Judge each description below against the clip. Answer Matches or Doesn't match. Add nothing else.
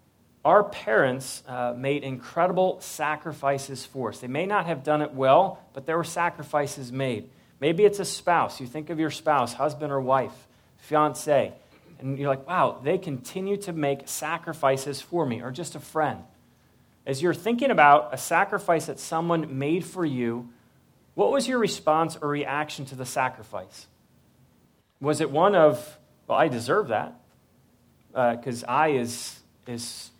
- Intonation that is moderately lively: Matches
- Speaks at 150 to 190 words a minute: Matches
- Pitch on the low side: Doesn't match